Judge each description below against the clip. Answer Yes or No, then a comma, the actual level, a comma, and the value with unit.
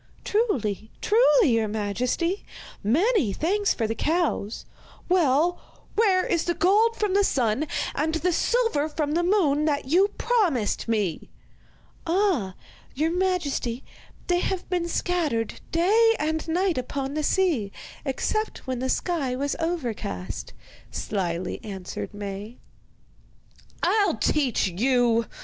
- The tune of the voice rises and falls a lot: Yes, wide, 8.0 semitones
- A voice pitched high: Yes, very high, 305 Hz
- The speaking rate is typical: No, slow, 125 wpm